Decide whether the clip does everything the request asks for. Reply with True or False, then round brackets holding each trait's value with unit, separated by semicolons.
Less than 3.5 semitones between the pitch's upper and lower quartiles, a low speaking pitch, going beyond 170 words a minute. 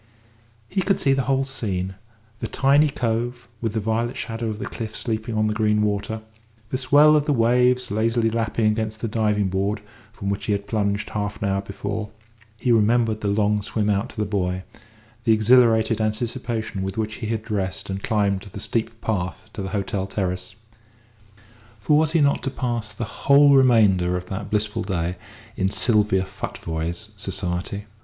True (2.8 semitones; 110 Hz; 180 wpm)